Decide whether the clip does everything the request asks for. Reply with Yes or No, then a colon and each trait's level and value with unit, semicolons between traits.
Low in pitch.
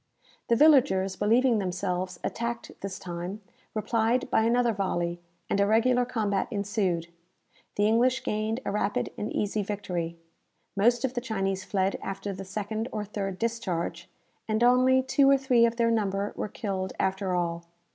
No: high, 210 Hz